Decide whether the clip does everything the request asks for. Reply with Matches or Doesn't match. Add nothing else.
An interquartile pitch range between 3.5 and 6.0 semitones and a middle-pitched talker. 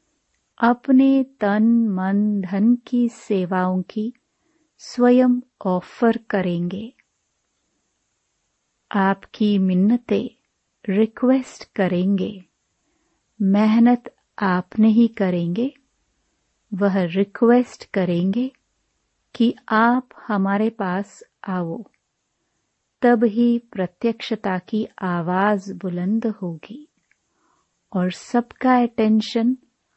Doesn't match